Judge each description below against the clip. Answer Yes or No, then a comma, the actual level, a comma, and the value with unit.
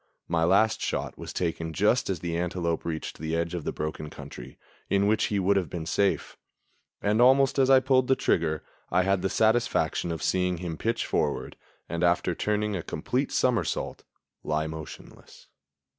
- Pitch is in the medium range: No, very low, 90 Hz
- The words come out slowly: No, average, 175 wpm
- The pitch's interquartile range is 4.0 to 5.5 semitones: Yes, average, 4.3 semitones